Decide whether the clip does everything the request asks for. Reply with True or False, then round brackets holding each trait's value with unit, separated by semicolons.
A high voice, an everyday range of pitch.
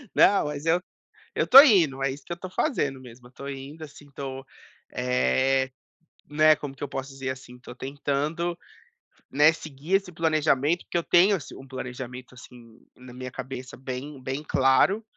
False (135 Hz; 3.2 semitones)